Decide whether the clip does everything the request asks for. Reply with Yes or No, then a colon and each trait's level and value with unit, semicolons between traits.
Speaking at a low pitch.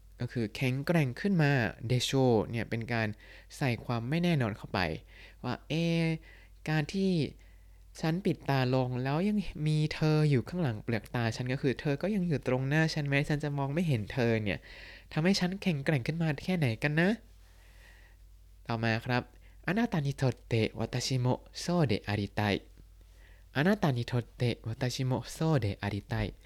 Yes: low, 130 Hz